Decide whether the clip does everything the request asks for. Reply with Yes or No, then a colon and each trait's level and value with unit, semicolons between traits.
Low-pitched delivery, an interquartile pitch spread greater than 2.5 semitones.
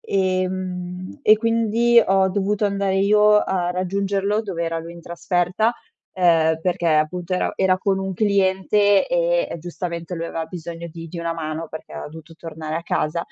No: medium, 180 Hz; average, 2.9 semitones